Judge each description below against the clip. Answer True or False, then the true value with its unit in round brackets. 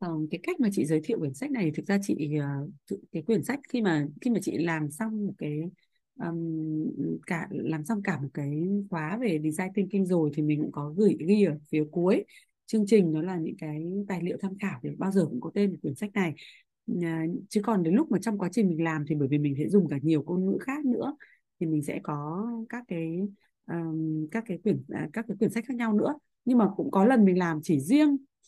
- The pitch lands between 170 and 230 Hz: True (185 Hz)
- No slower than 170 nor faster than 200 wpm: False (240 wpm)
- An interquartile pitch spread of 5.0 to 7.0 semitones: True (5.6 semitones)